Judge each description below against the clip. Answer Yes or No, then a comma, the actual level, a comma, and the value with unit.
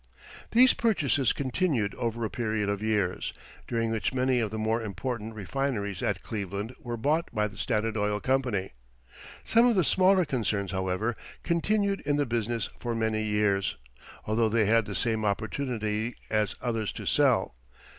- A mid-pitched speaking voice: No, low, 115 Hz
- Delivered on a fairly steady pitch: No, average, 3.9 semitones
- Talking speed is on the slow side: No, average, 160 wpm